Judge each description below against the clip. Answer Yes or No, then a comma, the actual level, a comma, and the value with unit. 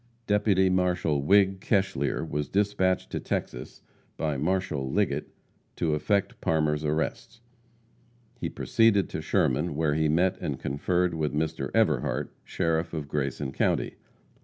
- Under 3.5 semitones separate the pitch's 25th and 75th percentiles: No, average, 4.2 semitones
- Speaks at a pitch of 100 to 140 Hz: No, very low, 80 Hz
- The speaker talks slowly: Yes, slow, 130 wpm